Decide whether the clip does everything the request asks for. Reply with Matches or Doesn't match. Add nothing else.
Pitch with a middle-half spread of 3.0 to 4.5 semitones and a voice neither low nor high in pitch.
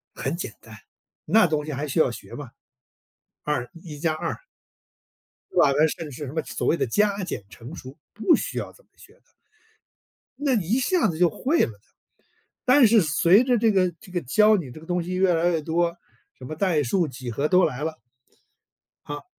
Doesn't match